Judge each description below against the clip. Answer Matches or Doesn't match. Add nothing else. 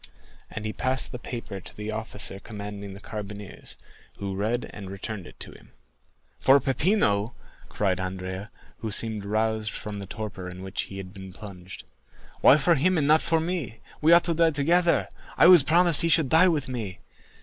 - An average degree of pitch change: Doesn't match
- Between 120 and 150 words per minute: Doesn't match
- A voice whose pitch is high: Doesn't match